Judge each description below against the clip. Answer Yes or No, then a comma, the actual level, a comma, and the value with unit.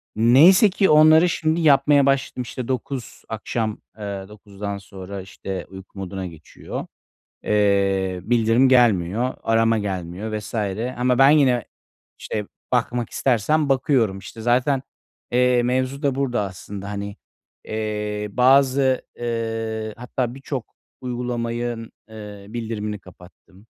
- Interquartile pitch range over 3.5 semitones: Yes, average, 4.0 semitones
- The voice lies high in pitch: No, low, 115 Hz